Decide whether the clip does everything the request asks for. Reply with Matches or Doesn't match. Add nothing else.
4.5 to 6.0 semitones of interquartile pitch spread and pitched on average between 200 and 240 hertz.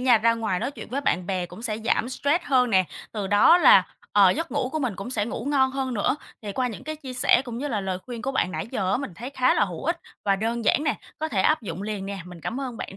Matches